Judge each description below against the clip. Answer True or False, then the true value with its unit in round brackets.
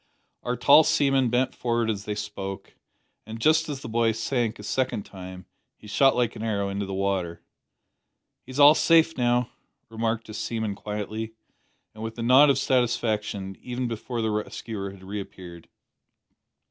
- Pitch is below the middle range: True (110 Hz)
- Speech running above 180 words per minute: False (160 wpm)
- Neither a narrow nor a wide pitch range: True (3.4 semitones)